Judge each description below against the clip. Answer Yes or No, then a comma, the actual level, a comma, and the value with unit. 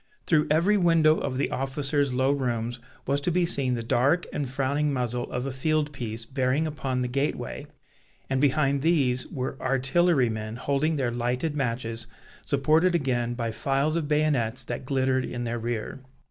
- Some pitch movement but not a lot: Yes, average, 3.3 semitones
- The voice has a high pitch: No, low, 135 Hz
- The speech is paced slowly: No, average, 165 wpm